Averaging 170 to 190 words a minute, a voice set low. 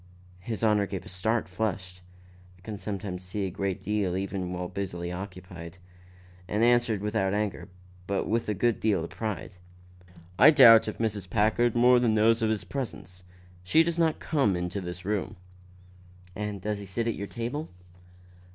Yes: average, 180 wpm; low, 105 Hz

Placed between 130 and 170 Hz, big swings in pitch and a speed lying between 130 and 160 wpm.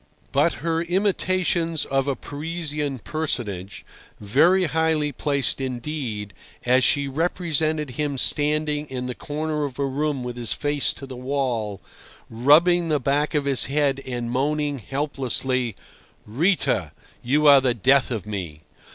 No: medium, 140 Hz; average, 3.3 semitones; average, 140 wpm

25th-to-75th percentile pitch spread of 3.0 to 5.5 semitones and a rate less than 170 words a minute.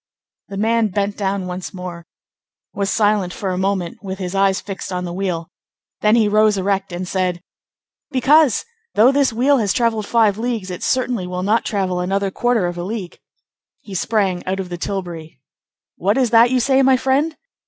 No: average, 3.8 semitones; average, 190 wpm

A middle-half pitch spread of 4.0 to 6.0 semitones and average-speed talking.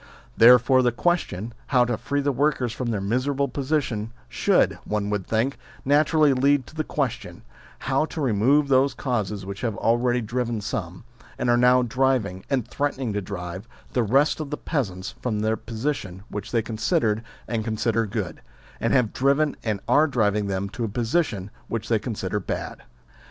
Yes: average, 4.5 semitones; average, 170 wpm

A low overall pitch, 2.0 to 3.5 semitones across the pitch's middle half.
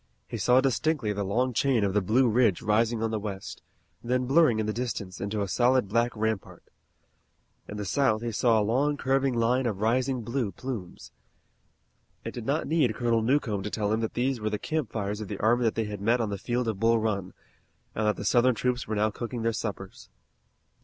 Yes: low, 115 Hz; average, 3.1 semitones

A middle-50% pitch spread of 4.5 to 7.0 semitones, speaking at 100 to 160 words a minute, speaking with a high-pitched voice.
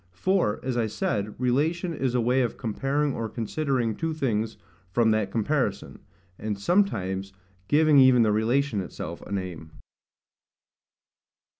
No: average, 5.1 semitones; average, 145 wpm; low, 120 Hz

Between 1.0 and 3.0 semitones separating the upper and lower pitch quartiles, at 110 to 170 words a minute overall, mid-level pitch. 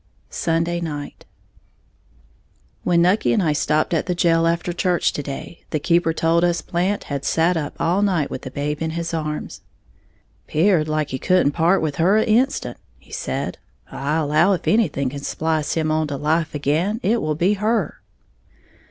No: average, 2.7 semitones; average, 180 wpm; medium, 165 Hz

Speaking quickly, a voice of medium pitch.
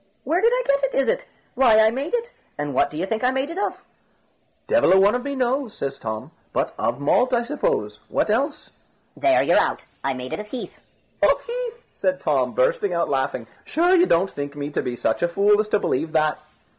No: fast, 230 wpm; very high, 250 Hz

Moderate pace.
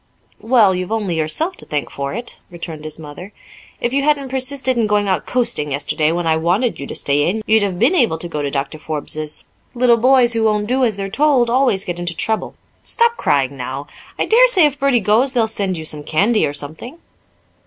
No: fast, 215 wpm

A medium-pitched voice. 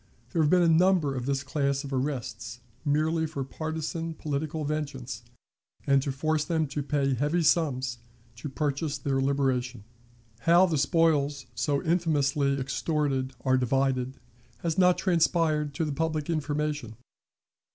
Yes: medium, 145 Hz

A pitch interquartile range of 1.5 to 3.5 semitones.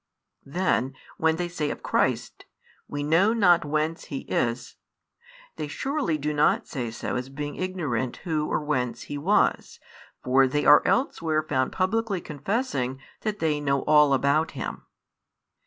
No: average, 4.2 semitones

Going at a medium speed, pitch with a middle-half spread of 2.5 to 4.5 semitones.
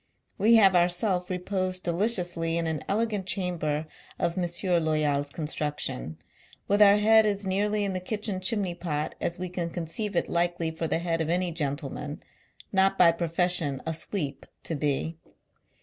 Yes: average, 165 wpm; average, 3.1 semitones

